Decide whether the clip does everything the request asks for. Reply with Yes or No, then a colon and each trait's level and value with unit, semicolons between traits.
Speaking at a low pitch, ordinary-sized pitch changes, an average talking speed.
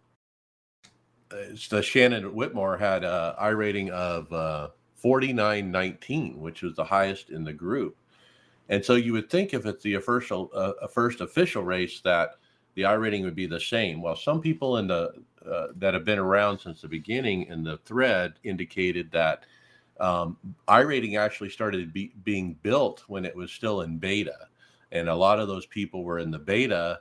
Yes: low, 100 Hz; average, 3.9 semitones; average, 185 wpm